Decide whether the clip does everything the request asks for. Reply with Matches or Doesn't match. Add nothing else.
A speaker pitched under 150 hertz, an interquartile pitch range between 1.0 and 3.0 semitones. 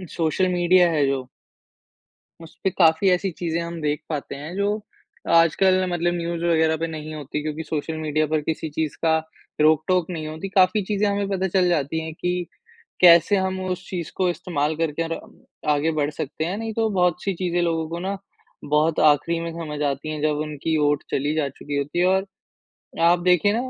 Doesn't match